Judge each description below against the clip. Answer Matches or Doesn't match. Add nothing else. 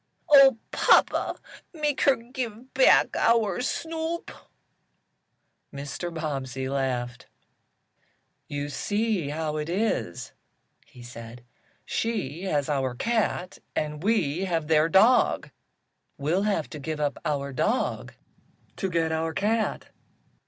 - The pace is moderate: Doesn't match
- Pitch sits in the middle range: Matches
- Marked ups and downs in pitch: Matches